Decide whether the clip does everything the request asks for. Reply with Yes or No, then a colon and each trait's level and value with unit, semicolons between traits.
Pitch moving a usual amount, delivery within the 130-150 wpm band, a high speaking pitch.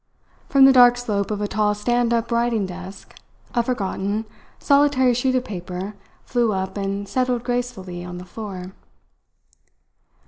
Yes: average, 4.1 semitones; average, 145 wpm; high, 215 Hz